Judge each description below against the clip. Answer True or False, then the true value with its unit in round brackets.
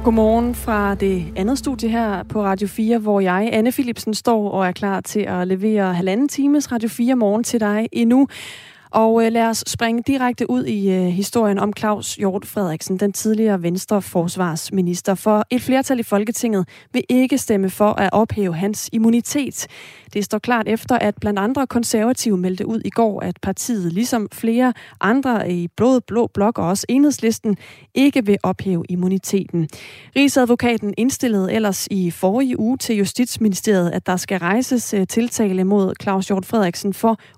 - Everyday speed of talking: True (165 wpm)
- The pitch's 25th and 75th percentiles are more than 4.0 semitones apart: False (3.5 semitones)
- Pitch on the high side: True (215 Hz)